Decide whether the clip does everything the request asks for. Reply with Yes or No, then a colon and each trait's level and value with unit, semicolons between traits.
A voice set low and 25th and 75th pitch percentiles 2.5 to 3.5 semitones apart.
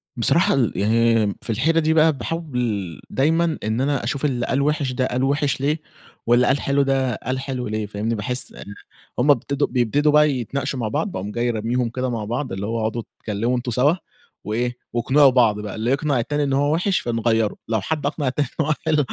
No: low, 125 Hz; average, 3.9 semitones